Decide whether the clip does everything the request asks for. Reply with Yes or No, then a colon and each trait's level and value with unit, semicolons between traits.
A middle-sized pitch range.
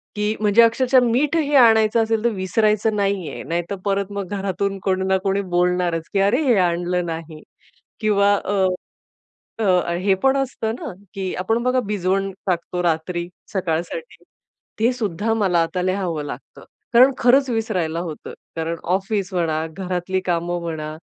Yes: average, 4.1 semitones